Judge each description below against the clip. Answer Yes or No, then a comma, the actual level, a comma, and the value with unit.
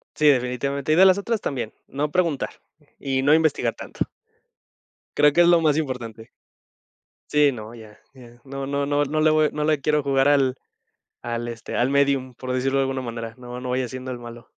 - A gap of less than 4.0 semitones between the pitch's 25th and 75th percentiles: Yes, average, 3.0 semitones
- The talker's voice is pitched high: No, low, 135 Hz